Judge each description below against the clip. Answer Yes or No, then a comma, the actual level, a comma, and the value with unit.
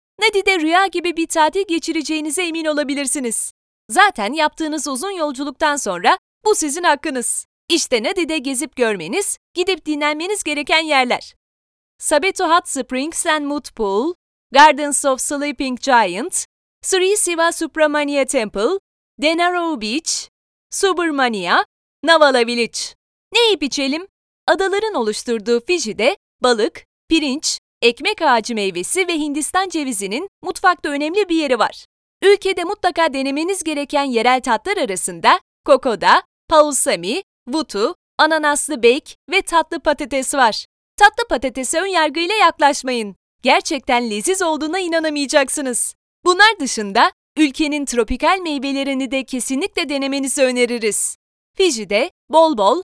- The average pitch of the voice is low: No, very high, 305 Hz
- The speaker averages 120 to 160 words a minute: No, average, 110 wpm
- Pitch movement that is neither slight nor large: Yes, average, 4.8 semitones